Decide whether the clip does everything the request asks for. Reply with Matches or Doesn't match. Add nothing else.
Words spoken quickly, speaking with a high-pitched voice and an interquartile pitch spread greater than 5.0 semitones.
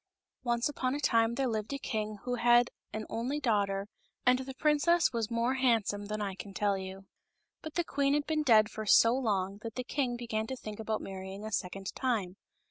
Doesn't match